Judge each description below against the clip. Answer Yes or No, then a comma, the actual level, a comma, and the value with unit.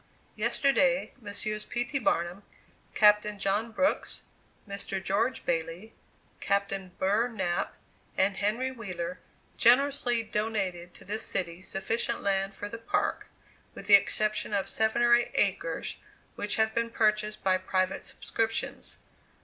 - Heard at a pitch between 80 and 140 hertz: No, high, 210 Hz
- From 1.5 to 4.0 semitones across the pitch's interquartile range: Yes, average, 3.0 semitones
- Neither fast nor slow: No, slow, 130 wpm